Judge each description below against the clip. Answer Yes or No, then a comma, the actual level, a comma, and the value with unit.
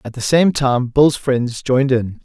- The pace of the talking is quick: Yes, fast, 215 wpm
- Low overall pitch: Yes, low, 130 Hz